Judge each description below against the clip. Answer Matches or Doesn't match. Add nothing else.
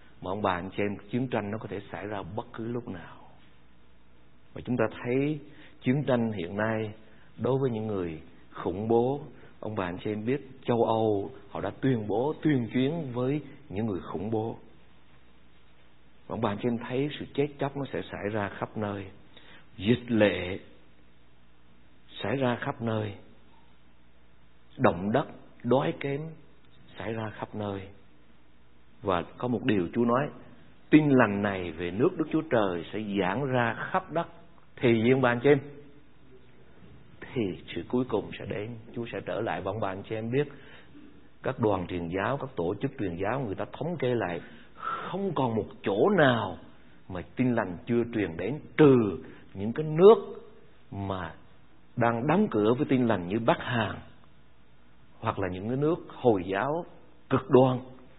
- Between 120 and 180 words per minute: Matches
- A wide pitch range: Matches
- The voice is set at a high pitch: Doesn't match